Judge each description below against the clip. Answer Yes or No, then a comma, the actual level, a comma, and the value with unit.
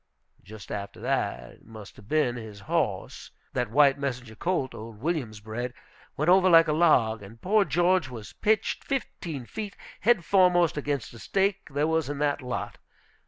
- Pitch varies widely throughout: Yes, wide, 7.6 semitones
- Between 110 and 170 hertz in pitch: Yes, medium, 140 Hz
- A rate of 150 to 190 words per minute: Yes, average, 170 wpm